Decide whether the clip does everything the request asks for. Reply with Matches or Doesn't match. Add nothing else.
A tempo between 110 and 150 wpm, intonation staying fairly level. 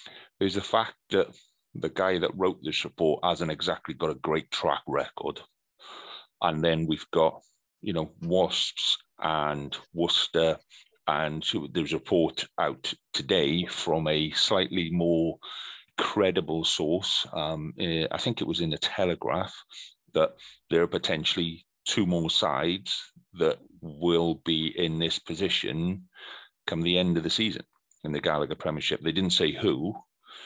Matches